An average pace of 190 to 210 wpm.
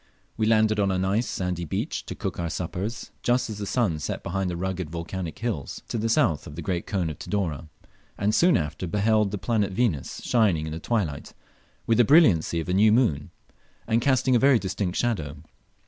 Yes: fast, 205 wpm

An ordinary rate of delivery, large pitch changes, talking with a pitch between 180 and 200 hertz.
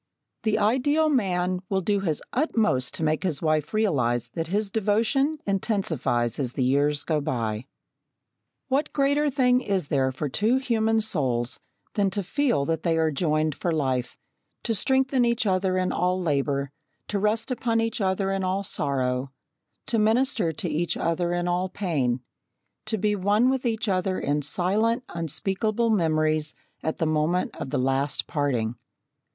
Yes: average, 160 wpm; wide, 6.6 semitones; medium, 185 Hz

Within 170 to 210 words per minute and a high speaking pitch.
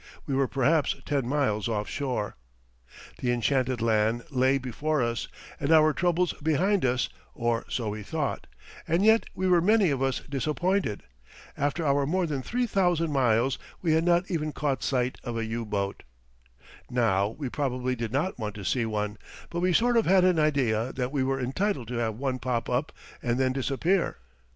No: average, 180 wpm; low, 135 Hz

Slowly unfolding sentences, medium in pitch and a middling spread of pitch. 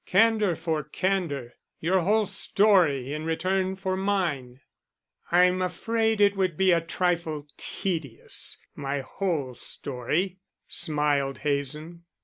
Yes: slow, 115 wpm; medium, 170 Hz; average, 4.7 semitones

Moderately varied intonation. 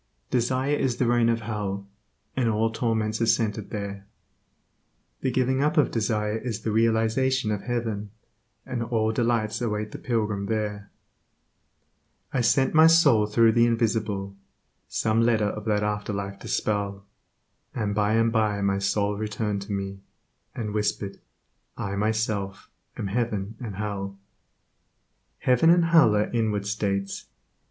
No: narrow, 2.3 semitones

